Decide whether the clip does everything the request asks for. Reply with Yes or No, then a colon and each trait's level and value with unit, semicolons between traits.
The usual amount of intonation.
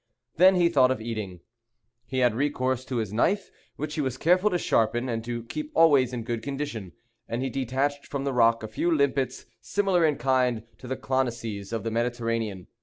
Yes: average, 3.7 semitones